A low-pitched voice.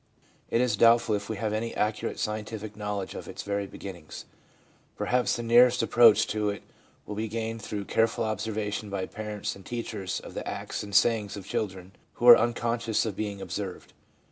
Yes: low, 105 Hz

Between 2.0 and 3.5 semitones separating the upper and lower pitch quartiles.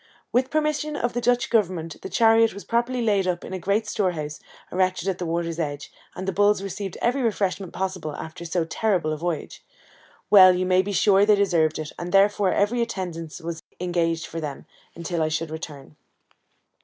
No: average, 3.9 semitones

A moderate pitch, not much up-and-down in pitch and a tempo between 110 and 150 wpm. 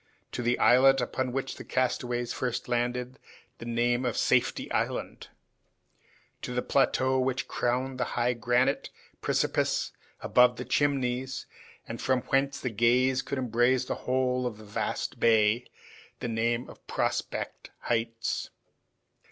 No: low, 125 Hz; narrow, 1.4 semitones; average, 140 wpm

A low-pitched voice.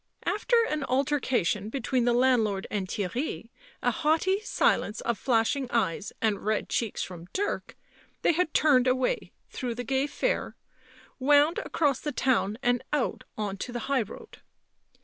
No: very high, 255 Hz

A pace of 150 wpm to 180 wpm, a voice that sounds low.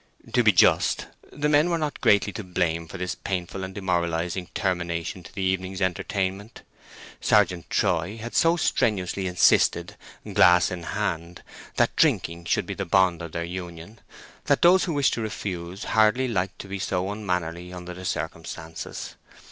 Yes: average, 165 wpm; very low, 95 Hz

